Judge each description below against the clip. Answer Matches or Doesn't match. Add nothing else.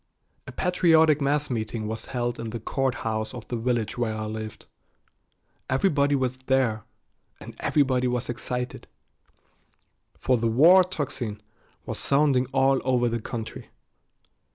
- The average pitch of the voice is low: Matches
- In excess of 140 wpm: Doesn't match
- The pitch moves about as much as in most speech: Matches